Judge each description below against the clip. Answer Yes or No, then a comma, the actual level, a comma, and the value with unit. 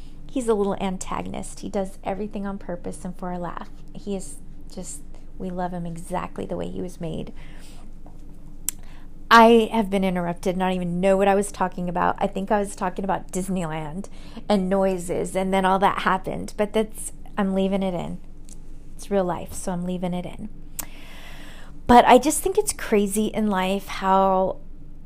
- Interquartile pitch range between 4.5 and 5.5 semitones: No, narrow, 2.5 semitones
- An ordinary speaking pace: Yes, average, 175 wpm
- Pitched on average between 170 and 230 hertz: Yes, high, 190 Hz